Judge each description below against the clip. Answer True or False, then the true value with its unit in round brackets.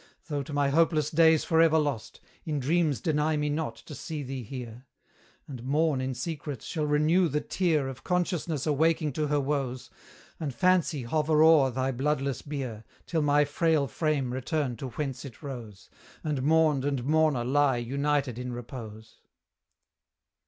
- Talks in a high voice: False (145 Hz)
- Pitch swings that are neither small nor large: True (3.2 semitones)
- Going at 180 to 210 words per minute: False (160 wpm)